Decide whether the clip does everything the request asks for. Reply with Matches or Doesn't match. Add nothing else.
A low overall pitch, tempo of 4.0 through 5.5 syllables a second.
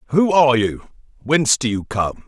Matches